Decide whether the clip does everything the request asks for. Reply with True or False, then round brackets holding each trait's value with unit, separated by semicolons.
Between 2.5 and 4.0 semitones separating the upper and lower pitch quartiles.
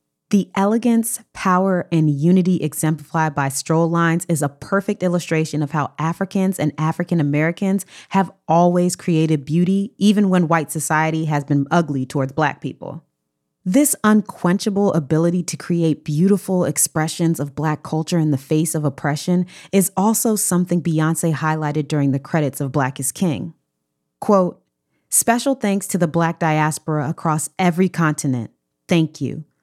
True (3.3 semitones)